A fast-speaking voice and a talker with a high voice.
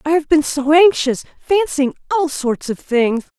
No: average, 175 wpm; very high, 295 Hz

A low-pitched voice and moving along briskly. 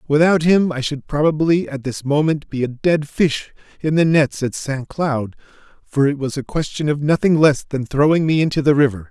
No: medium, 145 Hz; fast, 210 wpm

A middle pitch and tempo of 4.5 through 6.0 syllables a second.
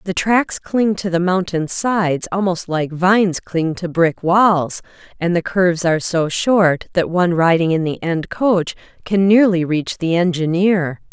No: medium, 180 Hz; 4.3 syllables/s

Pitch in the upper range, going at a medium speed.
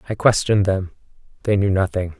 No: low, 100 Hz; average, 165 wpm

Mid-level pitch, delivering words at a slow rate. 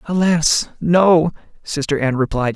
Yes: medium, 155 Hz; slow, 120 wpm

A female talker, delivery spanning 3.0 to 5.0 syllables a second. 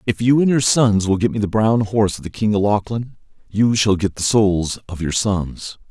No: male; 4.9 syllables/s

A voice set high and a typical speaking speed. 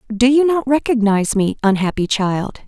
Yes: high, 230 Hz; average, 155 wpm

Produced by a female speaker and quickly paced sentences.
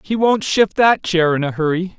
No: male; fast, 240 wpm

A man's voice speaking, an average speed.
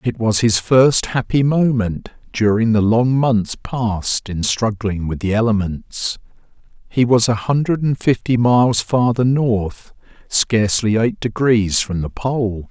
Yes: male; average, 145 wpm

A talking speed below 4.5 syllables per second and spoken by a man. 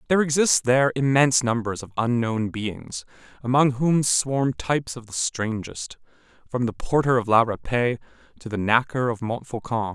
No: 4.9 syllables/s; male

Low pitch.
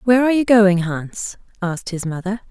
No: high, 200 Hz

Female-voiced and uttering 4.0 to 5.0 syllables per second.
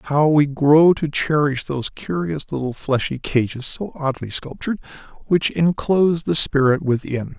No: male; 4.6 syllables/s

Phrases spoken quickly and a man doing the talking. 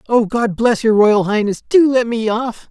Yes: fast, 220 wpm; male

